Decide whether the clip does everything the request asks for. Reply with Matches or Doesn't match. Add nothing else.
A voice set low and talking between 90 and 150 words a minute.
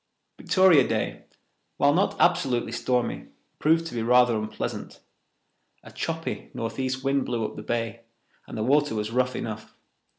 Matches